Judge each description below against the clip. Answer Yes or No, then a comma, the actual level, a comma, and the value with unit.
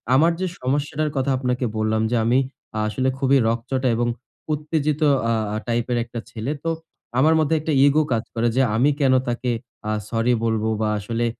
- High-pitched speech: No, low, 130 Hz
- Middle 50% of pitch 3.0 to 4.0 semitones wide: Yes, average, 3.6 semitones